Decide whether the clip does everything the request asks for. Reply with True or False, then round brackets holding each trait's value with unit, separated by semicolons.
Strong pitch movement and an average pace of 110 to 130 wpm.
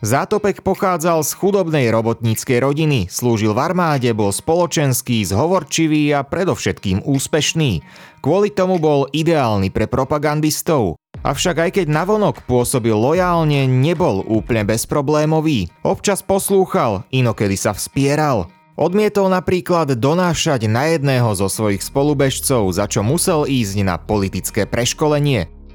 True (6.6 semitones; 120 wpm)